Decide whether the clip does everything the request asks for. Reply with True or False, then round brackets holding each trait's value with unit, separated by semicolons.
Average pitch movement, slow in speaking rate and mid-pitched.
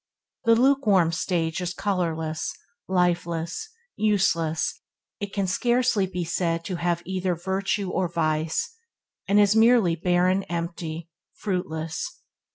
True (3.1 semitones; 115 wpm; 180 Hz)